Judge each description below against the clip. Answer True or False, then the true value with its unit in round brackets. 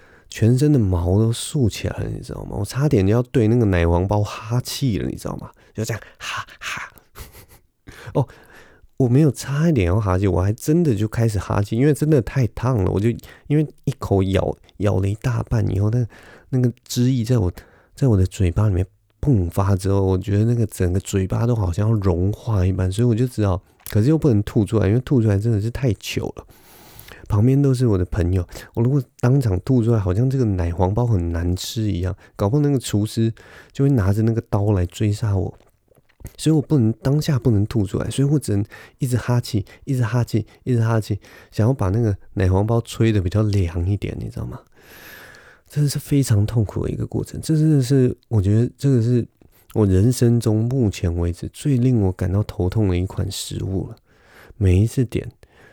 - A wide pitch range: False (4.2 semitones)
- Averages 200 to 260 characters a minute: False (295 characters per minute)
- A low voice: True (110 Hz)